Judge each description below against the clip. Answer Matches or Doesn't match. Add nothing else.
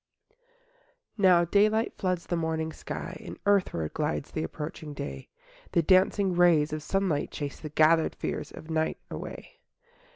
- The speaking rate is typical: Matches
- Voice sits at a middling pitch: Matches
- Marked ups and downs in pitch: Doesn't match